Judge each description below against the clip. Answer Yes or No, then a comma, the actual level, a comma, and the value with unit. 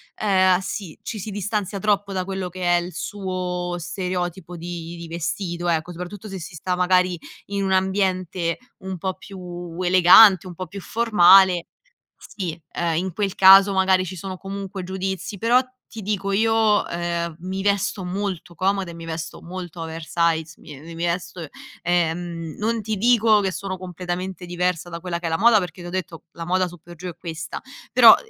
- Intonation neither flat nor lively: No, narrow, 2.0 semitones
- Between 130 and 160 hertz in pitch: No, medium, 185 Hz